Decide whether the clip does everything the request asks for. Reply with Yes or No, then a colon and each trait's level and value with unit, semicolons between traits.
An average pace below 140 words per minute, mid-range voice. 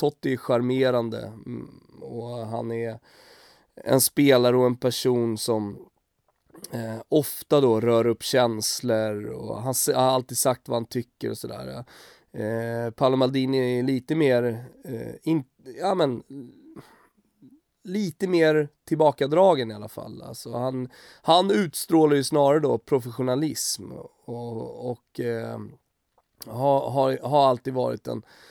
No: average, 130 wpm; low, 125 Hz